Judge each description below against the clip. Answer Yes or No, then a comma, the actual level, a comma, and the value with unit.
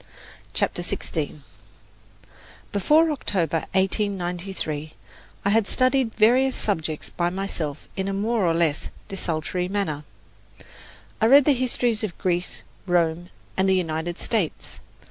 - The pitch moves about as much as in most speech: Yes, average, 4.6 semitones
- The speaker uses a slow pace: Yes, slow, 120 wpm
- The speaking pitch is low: No, high, 190 Hz